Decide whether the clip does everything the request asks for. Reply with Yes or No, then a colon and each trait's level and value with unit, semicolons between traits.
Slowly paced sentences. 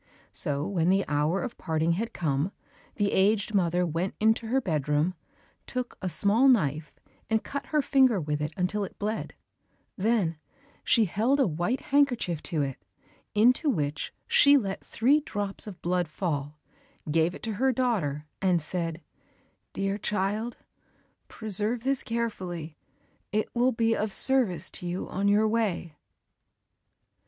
No: average, 145 wpm